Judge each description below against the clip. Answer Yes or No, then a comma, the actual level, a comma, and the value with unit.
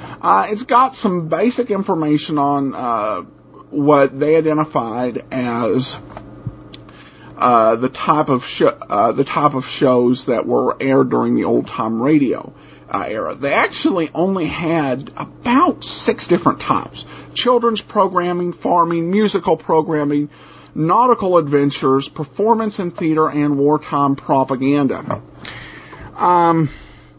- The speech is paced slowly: Yes, slow, 125 wpm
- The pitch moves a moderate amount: Yes, average, 4.9 semitones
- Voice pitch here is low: No, medium, 150 Hz